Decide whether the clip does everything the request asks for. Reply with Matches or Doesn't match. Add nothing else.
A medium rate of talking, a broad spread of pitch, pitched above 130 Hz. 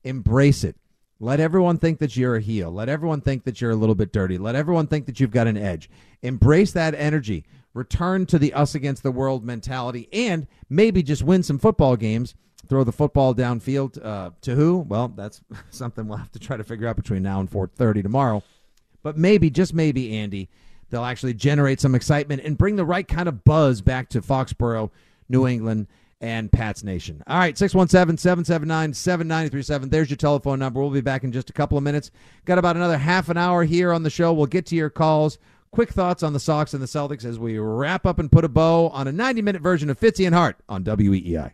Doesn't match